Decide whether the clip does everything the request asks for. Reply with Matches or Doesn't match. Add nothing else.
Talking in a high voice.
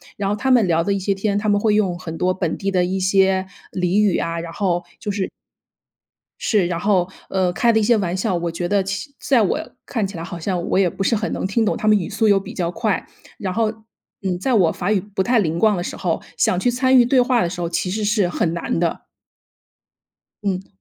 Matches